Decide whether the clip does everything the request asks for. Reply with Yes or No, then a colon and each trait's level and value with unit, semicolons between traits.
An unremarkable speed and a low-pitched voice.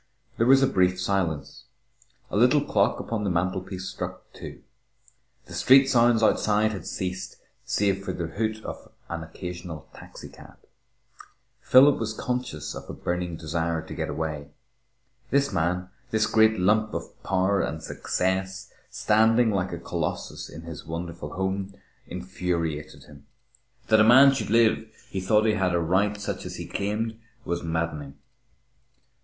Yes: average, 150 wpm; very low, 95 Hz